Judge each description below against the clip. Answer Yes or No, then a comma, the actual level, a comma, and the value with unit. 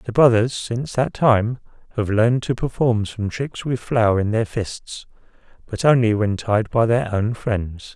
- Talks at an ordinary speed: Yes, average, 180 wpm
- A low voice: Yes, low, 115 Hz